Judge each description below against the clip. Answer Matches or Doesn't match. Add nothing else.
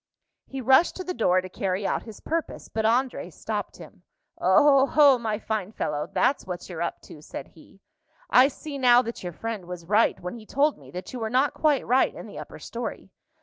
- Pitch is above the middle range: Matches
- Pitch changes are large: Matches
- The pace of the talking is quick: Matches